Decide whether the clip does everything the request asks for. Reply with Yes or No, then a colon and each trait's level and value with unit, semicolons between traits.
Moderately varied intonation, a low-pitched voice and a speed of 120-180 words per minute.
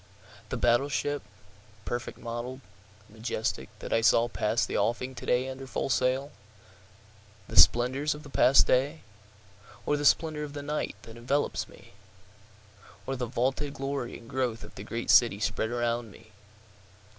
Yes: average, 3.5 semitones; low, 120 Hz; average, 150 wpm